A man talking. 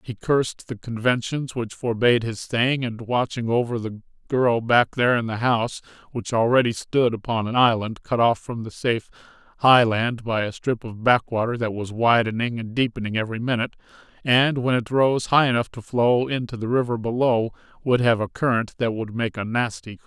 Yes: male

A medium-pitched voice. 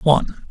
Yes: medium, 150 Hz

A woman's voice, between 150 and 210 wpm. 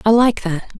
No: female; fast, 225 wpm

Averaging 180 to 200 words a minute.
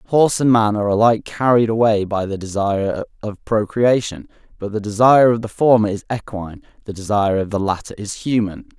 Yes: average, 185 wpm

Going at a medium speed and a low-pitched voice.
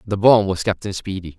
No: fast, 215 wpm; very low, 95 Hz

